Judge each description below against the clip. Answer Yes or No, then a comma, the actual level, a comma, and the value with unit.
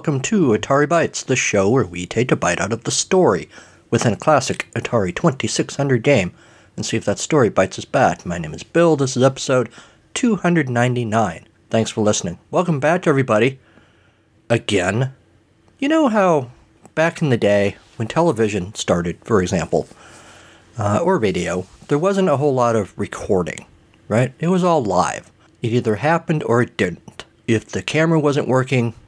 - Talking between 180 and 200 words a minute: No, average, 170 wpm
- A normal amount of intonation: No, wide, 6.1 semitones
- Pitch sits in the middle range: No, low, 125 Hz